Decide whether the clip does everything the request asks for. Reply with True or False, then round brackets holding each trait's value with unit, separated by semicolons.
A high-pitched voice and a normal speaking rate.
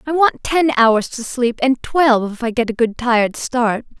False (250 Hz; 225 wpm)